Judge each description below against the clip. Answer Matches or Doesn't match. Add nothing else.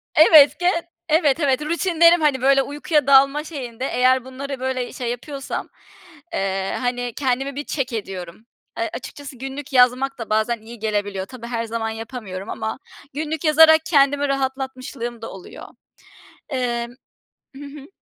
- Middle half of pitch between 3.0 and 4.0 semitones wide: Matches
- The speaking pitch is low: Doesn't match